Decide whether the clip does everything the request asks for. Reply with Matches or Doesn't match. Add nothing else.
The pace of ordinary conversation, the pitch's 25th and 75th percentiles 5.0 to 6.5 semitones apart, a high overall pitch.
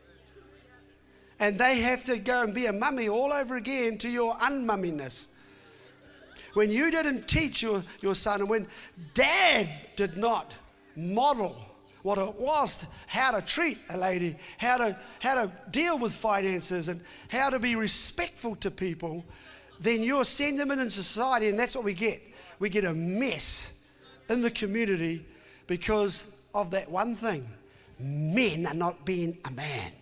Matches